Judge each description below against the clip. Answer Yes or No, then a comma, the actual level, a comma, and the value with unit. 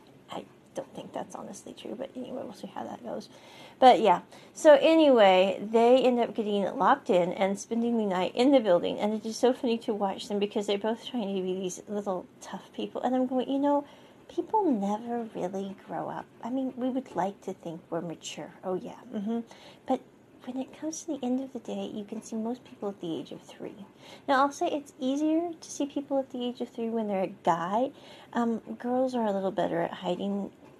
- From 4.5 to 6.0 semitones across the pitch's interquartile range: Yes, average, 4.8 semitones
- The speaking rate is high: Yes, fast, 220 wpm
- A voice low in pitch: No, high, 230 Hz